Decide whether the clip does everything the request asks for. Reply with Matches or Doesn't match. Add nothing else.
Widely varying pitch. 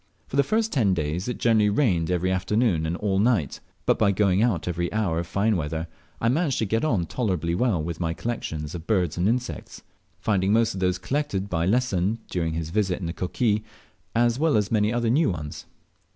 Doesn't match